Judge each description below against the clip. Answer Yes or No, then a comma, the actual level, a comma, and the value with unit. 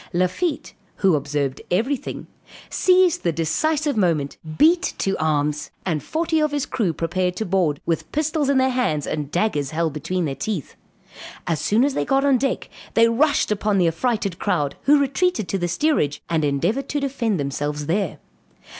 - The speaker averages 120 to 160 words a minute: No, average, 175 wpm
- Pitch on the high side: Yes, high, 195 Hz